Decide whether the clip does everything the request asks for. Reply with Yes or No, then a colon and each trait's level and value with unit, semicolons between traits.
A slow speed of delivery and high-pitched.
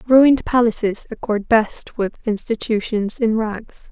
Yes: slow, 125 wpm; high, 225 Hz